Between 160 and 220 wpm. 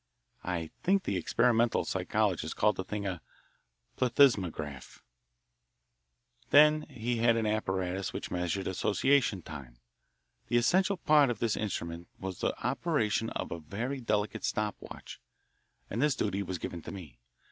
No: average, 140 wpm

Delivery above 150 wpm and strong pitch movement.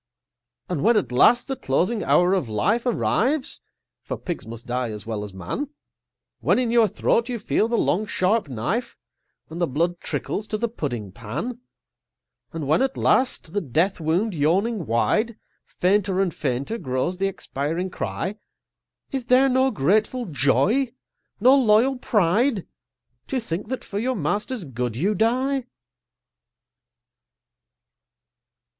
No: average, 145 wpm; wide, 8.4 semitones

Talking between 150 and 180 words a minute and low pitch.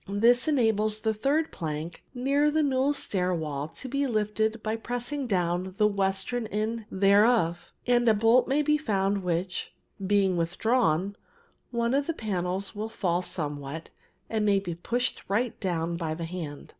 No: average, 160 wpm; high, 210 Hz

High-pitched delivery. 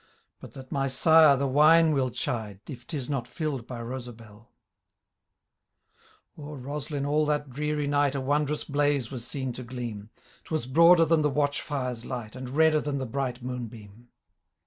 No: low, 135 Hz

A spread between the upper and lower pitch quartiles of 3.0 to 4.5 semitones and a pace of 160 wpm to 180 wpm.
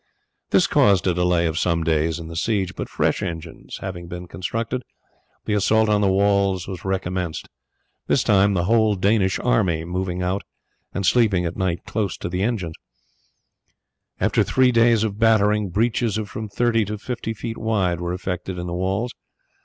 Yes: average, 3.7 semitones; average, 170 wpm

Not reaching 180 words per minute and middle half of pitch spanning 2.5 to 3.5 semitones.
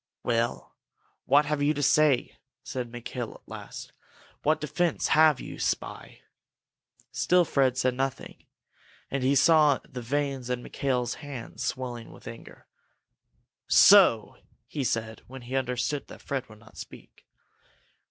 Yes: slow, 135 wpm; average, 3.0 semitones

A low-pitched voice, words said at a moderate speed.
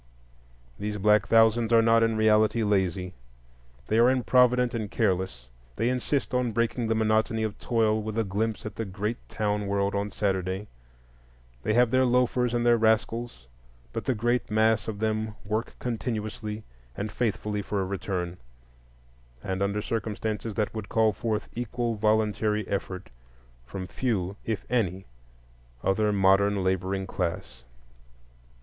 Yes: low, 110 Hz; average, 145 wpm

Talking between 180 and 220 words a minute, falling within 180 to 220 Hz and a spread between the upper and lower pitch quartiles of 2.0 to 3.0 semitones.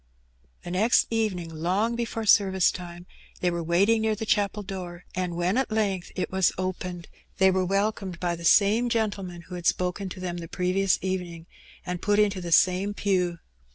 Yes: average, 185 wpm; medium, 185 Hz; average, 2.7 semitones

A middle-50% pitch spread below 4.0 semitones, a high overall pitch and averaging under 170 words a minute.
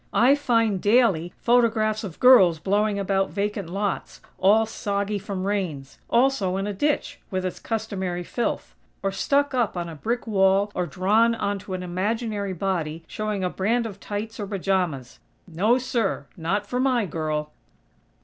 Yes: average, 3.3 semitones; high, 200 Hz; average, 160 wpm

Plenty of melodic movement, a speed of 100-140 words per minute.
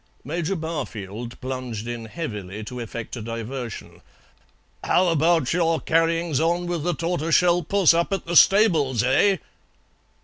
Yes: wide, 6.3 semitones; slow, 135 wpm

